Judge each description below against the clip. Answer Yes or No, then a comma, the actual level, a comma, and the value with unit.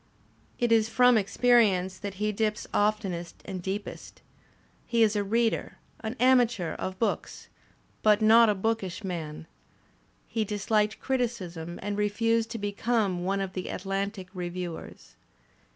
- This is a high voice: Yes, high, 205 Hz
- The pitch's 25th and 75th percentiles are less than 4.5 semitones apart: Yes, average, 3.3 semitones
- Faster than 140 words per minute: No, slow, 135 wpm